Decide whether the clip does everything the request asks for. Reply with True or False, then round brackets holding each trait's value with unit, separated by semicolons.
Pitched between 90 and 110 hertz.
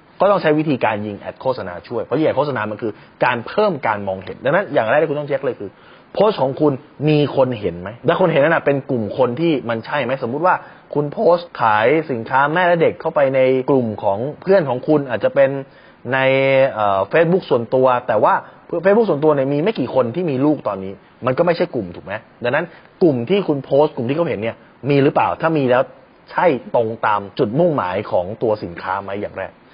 False (135 Hz)